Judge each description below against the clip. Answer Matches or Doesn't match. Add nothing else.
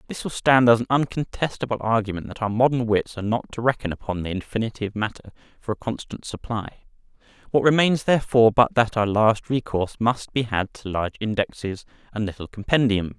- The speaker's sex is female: Doesn't match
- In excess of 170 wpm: Matches